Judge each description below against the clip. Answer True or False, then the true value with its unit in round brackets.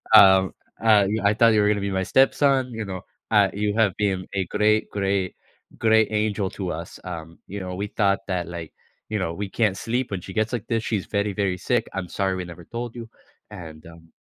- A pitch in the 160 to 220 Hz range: False (100 Hz)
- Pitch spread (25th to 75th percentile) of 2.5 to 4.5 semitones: True (2.8 semitones)